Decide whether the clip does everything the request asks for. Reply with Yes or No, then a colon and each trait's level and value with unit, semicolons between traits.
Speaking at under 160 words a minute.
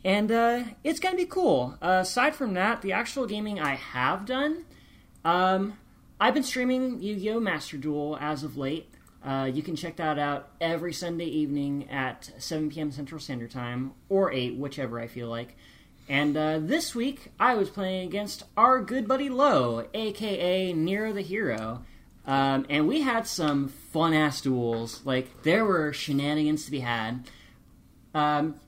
No: average, 165 wpm